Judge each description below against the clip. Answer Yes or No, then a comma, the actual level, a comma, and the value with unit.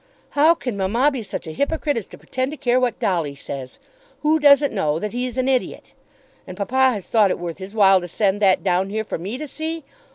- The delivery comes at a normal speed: No, fast, 230 wpm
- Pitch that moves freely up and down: Yes, wide, 5.9 semitones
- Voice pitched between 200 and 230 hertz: Yes, high, 225 Hz